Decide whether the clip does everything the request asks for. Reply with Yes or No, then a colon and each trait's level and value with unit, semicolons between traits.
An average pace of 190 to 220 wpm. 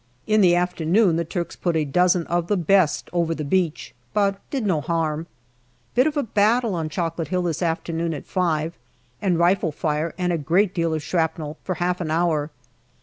Yes: average, 195 wpm